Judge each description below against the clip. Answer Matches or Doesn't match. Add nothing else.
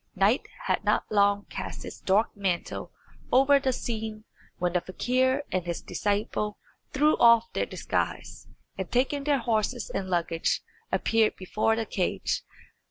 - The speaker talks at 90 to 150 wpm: Matches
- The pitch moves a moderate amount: Matches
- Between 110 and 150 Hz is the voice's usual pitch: Doesn't match